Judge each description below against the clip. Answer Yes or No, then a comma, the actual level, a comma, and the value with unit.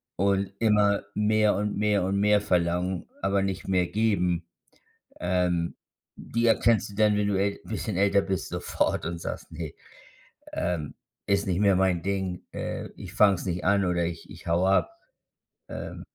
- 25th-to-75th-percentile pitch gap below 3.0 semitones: Yes, narrow, 2.5 semitones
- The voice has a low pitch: Yes, very low, 95 Hz